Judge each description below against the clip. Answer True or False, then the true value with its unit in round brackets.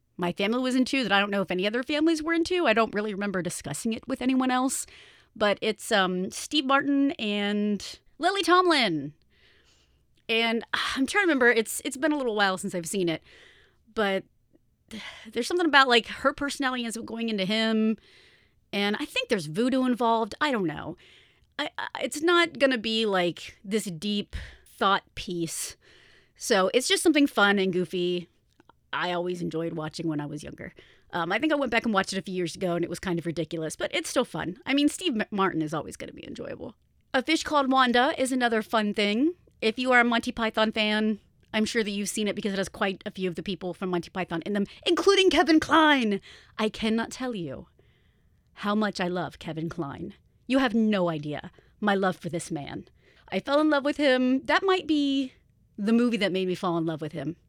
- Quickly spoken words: True (210 wpm)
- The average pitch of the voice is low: False (220 Hz)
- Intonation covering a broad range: True (6.2 semitones)